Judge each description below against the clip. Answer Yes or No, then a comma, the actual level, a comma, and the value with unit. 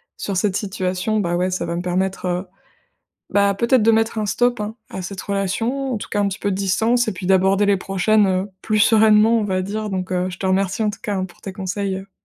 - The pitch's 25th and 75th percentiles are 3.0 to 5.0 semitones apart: No, narrow, 2.5 semitones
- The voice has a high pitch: Yes, high, 195 Hz